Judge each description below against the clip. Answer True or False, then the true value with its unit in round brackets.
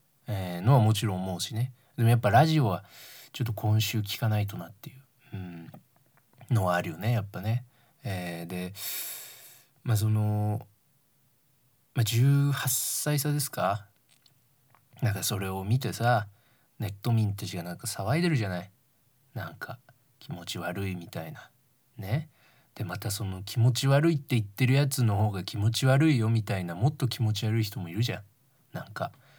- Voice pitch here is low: True (115 Hz)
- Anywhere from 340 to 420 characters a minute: False (305 characters per minute)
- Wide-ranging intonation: False (4.2 semitones)